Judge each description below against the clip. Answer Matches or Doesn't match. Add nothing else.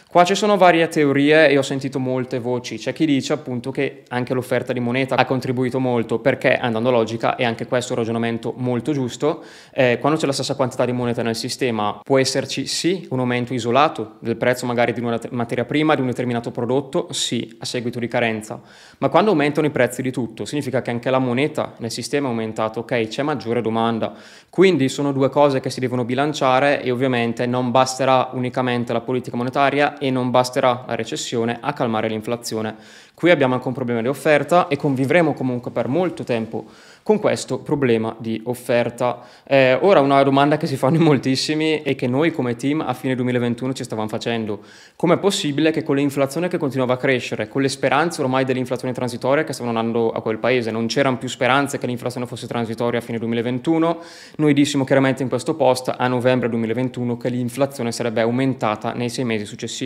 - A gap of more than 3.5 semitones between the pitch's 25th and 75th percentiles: Doesn't match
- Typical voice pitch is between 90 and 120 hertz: Doesn't match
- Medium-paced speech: Doesn't match